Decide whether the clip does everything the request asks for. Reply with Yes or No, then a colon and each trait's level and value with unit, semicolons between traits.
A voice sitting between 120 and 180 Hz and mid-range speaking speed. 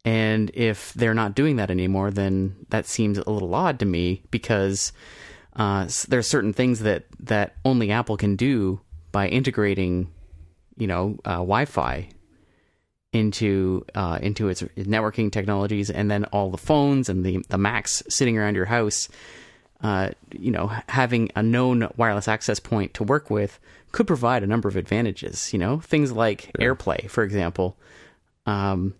No: low, 105 Hz; average, 165 wpm